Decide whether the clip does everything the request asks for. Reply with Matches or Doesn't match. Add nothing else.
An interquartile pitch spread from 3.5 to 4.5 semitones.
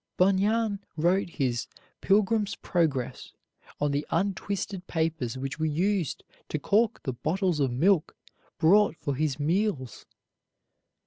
Doesn't match